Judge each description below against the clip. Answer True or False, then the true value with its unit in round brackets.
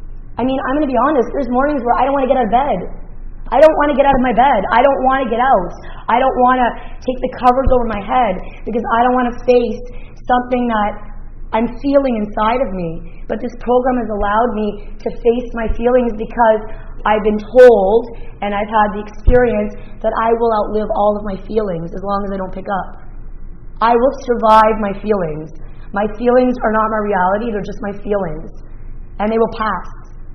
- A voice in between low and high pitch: False (225 Hz)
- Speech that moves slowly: False (215 wpm)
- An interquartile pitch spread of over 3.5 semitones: False (3.2 semitones)